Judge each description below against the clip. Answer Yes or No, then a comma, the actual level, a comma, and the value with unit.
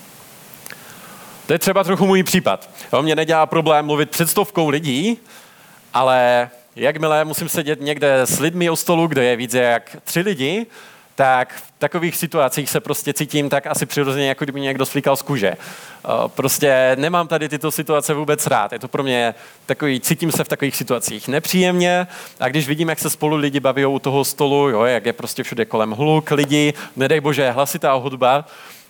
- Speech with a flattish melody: No, average, 3.2 semitones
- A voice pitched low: No, medium, 150 Hz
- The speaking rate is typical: No, fast, 180 wpm